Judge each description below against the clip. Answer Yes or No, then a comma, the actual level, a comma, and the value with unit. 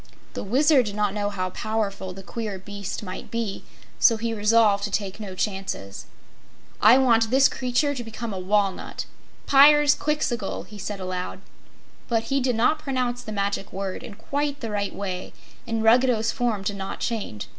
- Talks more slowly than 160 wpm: No, average, 170 wpm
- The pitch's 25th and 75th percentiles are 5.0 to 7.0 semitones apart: No, average, 3.6 semitones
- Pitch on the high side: Yes, high, 215 Hz